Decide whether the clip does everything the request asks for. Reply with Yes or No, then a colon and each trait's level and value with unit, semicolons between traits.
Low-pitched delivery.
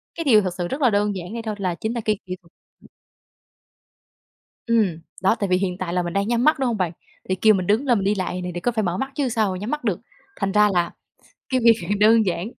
No: high, 205 Hz